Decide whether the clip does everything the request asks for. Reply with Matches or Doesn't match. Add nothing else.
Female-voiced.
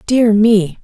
Matches